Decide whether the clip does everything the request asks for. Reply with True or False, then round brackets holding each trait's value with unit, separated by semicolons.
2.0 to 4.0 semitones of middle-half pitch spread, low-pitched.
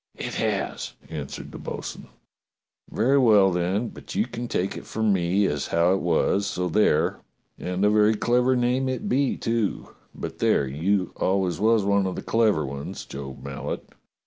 False (4.6 semitones; 100 Hz)